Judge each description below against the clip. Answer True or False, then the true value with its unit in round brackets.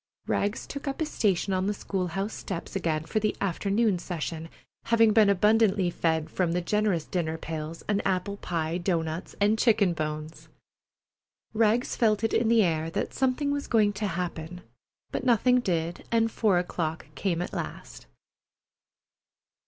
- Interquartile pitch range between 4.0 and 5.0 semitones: True (4.5 semitones)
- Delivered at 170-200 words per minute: False (160 wpm)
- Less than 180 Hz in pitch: False (195 Hz)